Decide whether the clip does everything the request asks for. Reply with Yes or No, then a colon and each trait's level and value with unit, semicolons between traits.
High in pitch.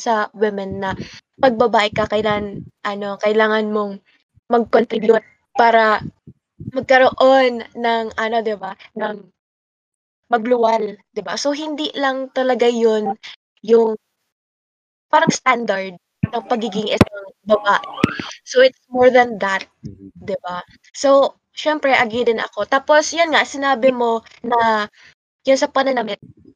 Yes: high, 225 Hz